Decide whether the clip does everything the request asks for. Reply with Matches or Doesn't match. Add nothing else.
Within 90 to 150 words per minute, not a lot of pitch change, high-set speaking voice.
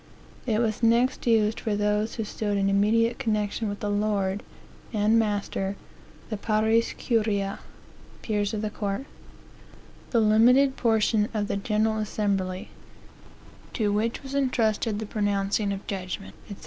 Matches